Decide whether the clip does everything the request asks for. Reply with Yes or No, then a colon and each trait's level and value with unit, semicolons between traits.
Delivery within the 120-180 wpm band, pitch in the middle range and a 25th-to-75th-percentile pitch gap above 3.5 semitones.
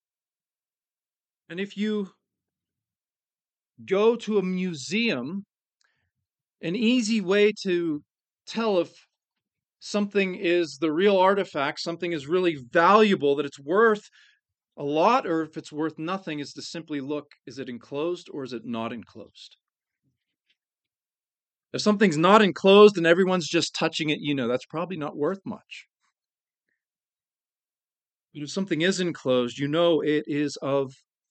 Yes: slow, 135 wpm; medium, 170 Hz; average, 5.1 semitones